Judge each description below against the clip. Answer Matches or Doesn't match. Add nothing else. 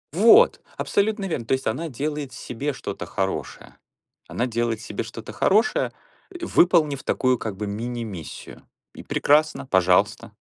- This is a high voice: Doesn't match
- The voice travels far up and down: Matches